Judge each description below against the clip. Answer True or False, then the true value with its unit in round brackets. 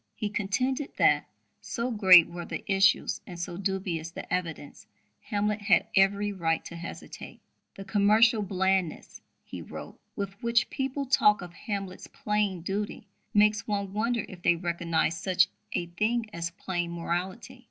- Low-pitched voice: False (195 Hz)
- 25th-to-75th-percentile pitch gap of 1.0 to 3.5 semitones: True (3.2 semitones)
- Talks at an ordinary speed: True (150 wpm)